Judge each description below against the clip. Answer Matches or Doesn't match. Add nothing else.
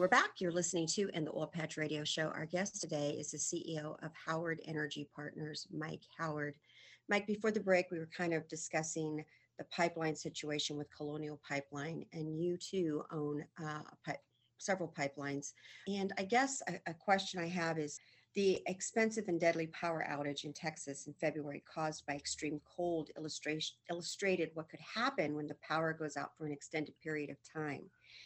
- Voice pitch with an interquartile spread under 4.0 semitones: Matches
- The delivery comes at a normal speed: Matches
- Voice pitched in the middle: Matches